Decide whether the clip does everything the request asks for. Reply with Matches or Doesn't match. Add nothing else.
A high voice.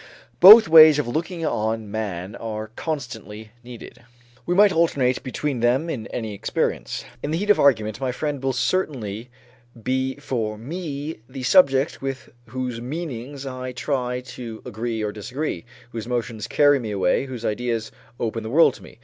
Doesn't match